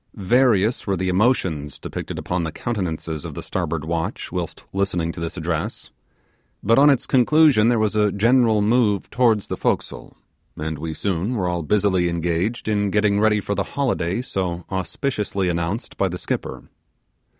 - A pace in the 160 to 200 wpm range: Yes, average, 165 wpm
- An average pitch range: Yes, average, 4.5 semitones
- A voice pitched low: Yes, low, 100 Hz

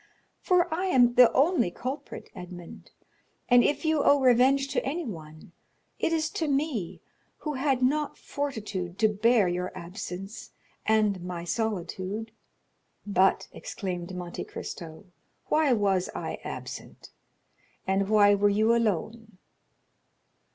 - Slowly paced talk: Yes, slow, 125 wpm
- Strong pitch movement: Yes, wide, 6.6 semitones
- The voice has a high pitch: Yes, high, 220 Hz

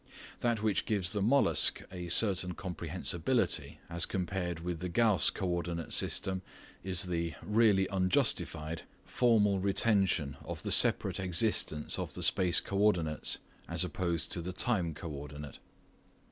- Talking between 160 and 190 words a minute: No, average, 140 wpm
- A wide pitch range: No, average, 3.0 semitones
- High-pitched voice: No, very low, 90 Hz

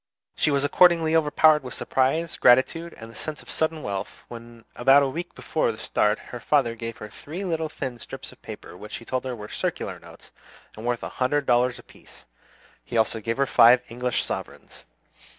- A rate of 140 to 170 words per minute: No, average, 195 wpm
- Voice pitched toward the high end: No, low, 130 Hz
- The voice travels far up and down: No, average, 4.7 semitones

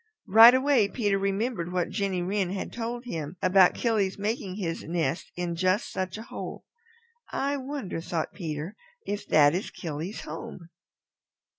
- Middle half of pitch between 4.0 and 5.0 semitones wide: Yes, average, 4.5 semitones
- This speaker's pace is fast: No, average, 150 wpm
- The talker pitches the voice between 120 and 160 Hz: No, high, 190 Hz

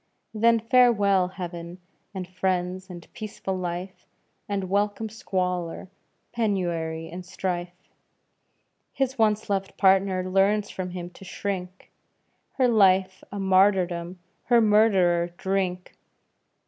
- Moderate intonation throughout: No, narrow, 2.3 semitones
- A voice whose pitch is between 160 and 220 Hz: Yes, high, 190 Hz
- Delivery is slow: Yes, slow, 110 wpm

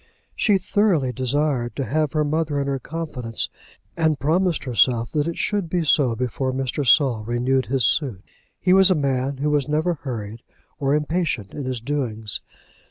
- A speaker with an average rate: Yes, average, 170 wpm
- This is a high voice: No, medium, 140 Hz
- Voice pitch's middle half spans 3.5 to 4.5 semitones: Yes, average, 3.9 semitones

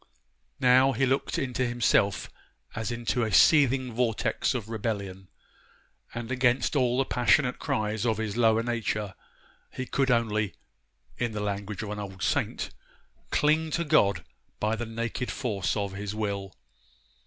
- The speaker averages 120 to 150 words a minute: Yes, average, 145 wpm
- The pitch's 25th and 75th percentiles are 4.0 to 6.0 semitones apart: No, average, 3.2 semitones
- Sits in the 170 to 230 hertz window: No, low, 115 Hz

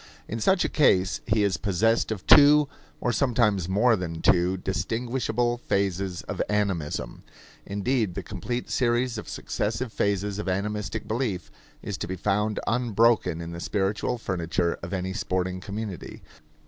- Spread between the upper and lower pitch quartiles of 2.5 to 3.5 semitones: No, average, 4.0 semitones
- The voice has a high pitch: No, low, 105 Hz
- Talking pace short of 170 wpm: Yes, average, 150 wpm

